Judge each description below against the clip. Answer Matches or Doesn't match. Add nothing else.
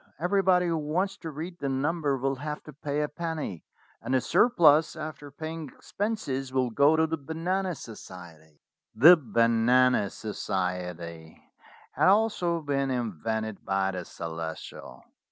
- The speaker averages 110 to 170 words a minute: Matches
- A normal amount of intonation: Doesn't match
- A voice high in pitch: Doesn't match